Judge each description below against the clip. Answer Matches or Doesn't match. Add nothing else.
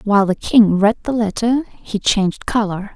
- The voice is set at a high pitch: Matches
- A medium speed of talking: Matches